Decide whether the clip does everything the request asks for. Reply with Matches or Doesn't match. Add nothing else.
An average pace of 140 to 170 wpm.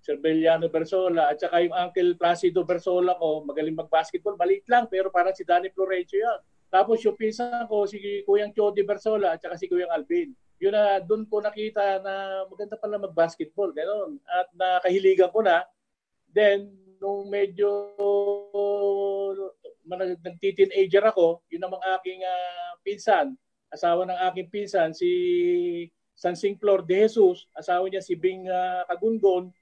Matches